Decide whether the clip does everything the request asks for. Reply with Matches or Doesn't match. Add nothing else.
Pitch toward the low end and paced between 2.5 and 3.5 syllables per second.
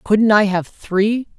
Doesn't match